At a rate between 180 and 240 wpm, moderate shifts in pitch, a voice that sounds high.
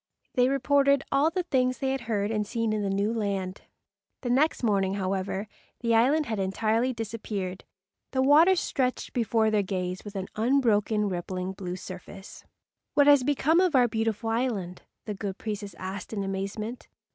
No: average, 170 wpm; average, 4.6 semitones; high, 220 Hz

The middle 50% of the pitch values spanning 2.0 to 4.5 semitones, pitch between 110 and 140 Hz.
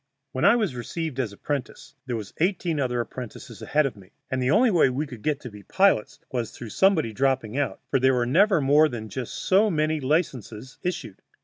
No: average, 4.9 semitones; low, 135 Hz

